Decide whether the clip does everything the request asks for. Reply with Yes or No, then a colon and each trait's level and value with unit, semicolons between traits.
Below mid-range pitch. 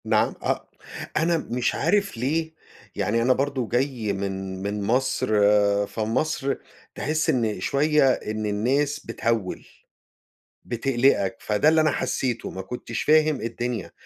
Yes: low, 125 Hz